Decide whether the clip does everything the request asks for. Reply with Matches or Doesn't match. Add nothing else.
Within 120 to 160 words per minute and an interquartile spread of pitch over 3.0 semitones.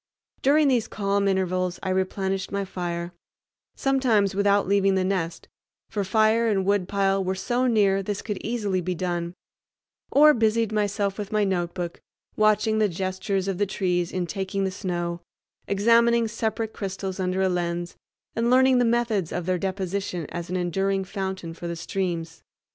Doesn't match